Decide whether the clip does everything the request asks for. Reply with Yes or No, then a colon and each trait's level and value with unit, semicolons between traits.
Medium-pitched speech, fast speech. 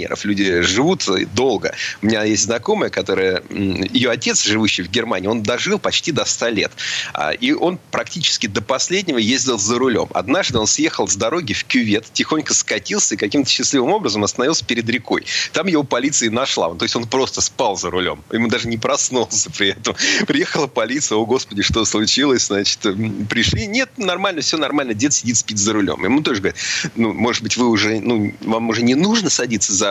No: low, 115 Hz; fast, 185 wpm